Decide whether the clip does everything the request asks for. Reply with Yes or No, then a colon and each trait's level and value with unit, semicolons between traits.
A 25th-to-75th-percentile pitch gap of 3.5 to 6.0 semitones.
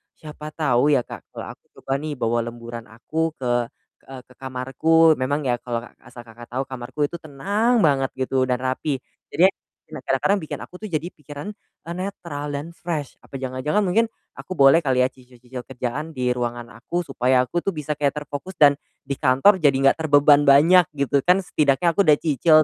Yes: average, 4.0 semitones